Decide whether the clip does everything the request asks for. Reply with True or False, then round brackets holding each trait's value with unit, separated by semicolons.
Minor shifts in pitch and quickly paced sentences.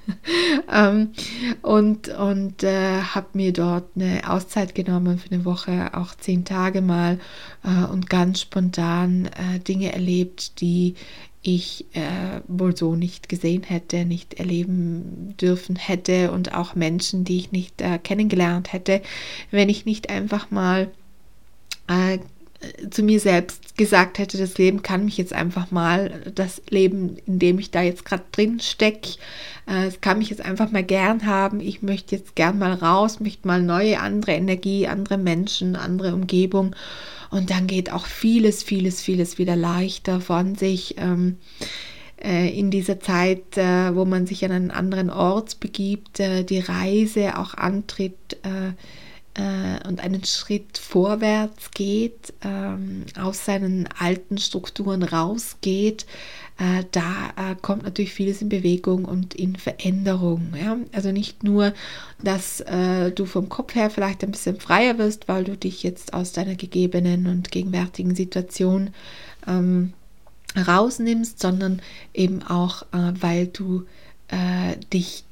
False (1.7 semitones; 145 wpm)